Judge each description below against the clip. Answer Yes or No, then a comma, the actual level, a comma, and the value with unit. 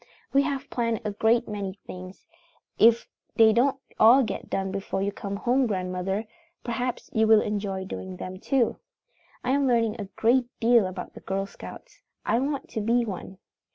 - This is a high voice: Yes, high, 220 Hz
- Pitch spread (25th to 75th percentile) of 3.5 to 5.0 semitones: Yes, average, 3.9 semitones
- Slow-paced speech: No, average, 175 wpm